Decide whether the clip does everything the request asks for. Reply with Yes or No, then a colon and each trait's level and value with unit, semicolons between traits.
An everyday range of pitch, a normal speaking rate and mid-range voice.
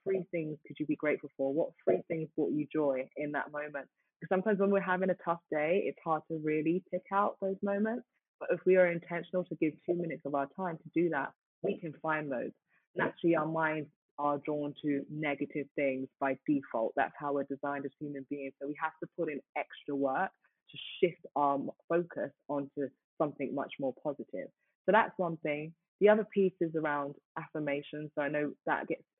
No: average, 3.2 semitones; fast, 210 wpm; medium, 155 Hz